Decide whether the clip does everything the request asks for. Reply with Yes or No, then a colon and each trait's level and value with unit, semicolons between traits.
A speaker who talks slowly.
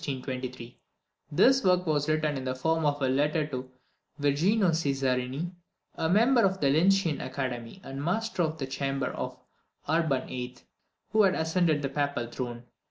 No: average, 160 wpm